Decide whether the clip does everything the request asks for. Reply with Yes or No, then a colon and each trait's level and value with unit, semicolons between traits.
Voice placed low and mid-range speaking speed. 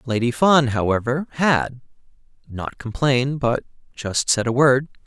No: low, 130 Hz; slow, 120 wpm